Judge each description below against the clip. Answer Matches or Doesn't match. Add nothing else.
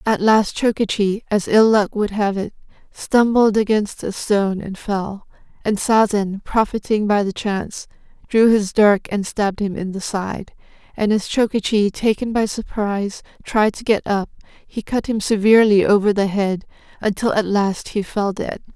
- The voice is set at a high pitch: Matches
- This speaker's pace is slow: Doesn't match